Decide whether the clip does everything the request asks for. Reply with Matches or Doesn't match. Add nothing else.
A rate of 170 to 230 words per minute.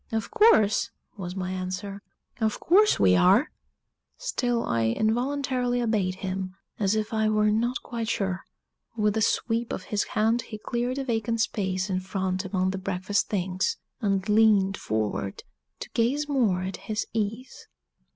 Doesn't match